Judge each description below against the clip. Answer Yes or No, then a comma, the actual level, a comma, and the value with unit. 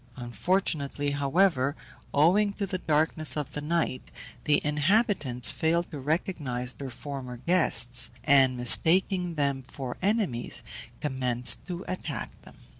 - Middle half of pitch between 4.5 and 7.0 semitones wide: Yes, average, 5.3 semitones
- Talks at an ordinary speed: No, slow, 120 wpm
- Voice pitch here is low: No, medium, 145 Hz